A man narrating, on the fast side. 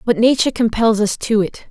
No: female; fast, 210 wpm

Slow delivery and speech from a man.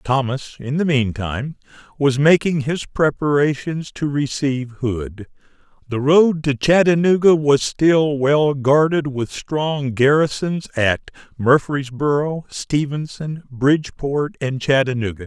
Yes: slow, 110 wpm; male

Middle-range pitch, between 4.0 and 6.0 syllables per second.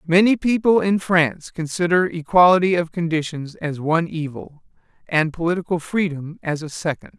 Yes: medium, 170 Hz; 5.2 syllables/s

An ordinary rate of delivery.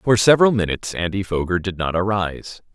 Yes: average, 175 wpm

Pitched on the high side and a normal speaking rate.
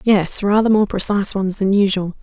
Yes: high, 200 Hz; average, 190 wpm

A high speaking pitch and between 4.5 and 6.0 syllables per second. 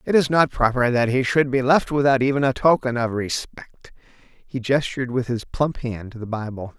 No: low, 125 Hz; 5.1 syllables/s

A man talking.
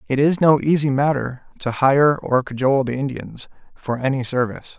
Yes: male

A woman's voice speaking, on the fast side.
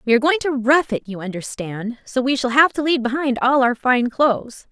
Yes: female; fast, 240 wpm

